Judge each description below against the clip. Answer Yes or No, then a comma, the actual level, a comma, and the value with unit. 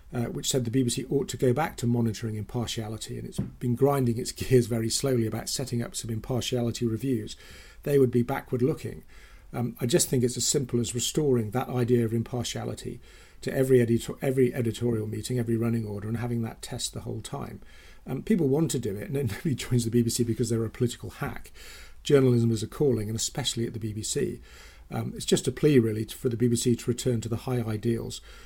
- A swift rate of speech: Yes, fast, 215 wpm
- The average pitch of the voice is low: Yes, low, 120 Hz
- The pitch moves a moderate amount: No, narrow, 2.0 semitones